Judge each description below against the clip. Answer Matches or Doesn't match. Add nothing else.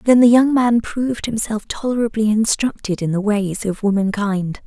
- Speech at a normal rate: Matches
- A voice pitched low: Doesn't match